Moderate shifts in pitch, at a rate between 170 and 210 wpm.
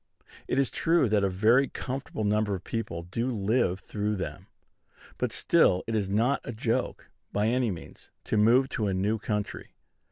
Yes: average, 3.1 semitones; average, 180 wpm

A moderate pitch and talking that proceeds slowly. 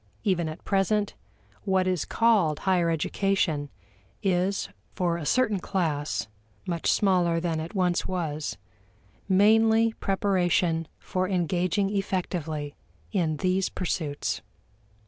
Yes: medium, 180 Hz; slow, 105 wpm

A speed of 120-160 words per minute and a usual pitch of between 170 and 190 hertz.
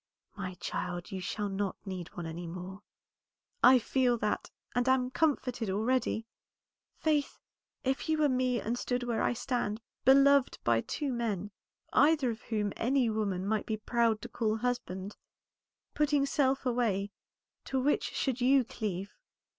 No: average, 150 wpm; high, 235 Hz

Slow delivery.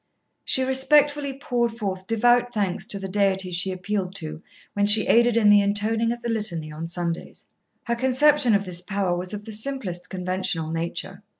No: average, 180 wpm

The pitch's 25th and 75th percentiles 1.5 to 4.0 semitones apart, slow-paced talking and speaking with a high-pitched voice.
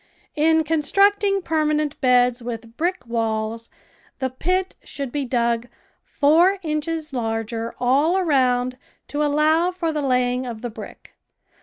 No: average, 4.8 semitones; slow, 130 wpm; very high, 280 Hz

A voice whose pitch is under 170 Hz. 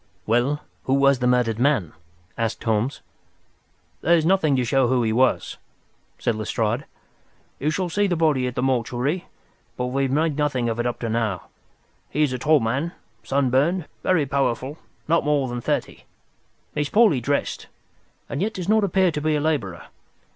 Yes: low, 135 Hz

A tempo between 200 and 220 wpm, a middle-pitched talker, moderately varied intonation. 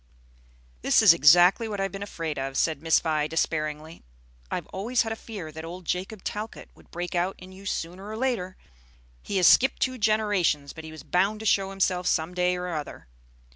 Yes: fast, 205 wpm; medium, 180 Hz; average, 4.1 semitones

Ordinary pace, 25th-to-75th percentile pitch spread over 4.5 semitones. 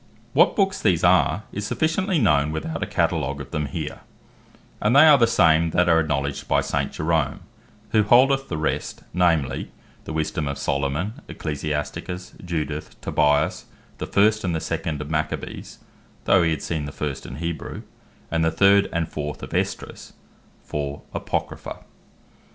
Yes: average, 155 wpm; average, 5.1 semitones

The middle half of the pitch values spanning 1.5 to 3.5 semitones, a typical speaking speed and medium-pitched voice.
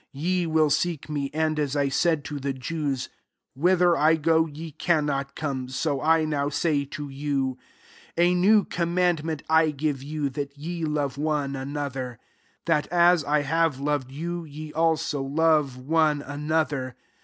Yes: narrow, 2.5 semitones; average, 165 wpm; medium, 150 Hz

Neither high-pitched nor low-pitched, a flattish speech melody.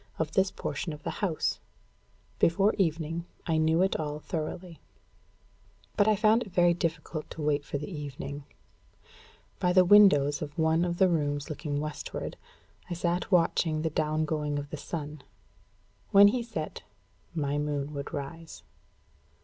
No: medium, 160 Hz; average, 3.0 semitones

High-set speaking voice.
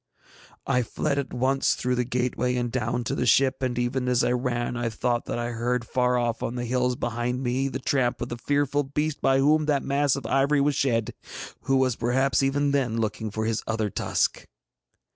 No: low, 125 Hz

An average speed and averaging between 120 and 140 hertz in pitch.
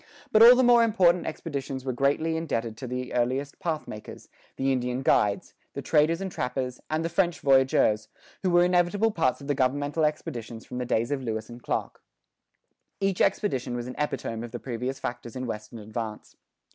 Yes: average, 180 wpm; low, 135 Hz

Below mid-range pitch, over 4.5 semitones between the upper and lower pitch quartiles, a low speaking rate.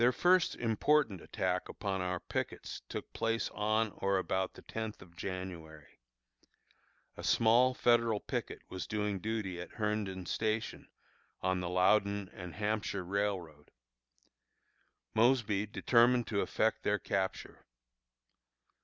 No: low, 105 Hz; average, 3.2 semitones; slow, 120 wpm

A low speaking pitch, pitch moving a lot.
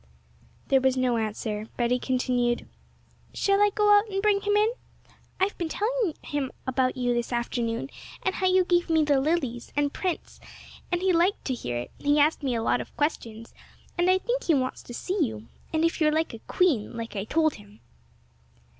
No: very high, 290 Hz; wide, 7.4 semitones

